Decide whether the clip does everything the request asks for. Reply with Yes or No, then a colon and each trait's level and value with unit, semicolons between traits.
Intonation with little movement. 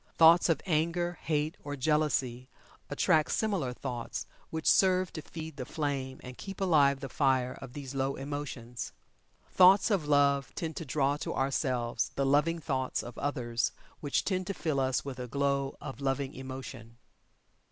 No: average, 3.3 semitones